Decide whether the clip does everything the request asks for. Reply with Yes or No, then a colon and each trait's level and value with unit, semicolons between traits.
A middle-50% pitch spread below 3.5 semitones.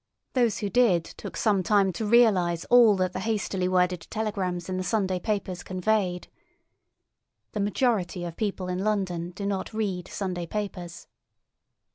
Yes: average, 2.9 semitones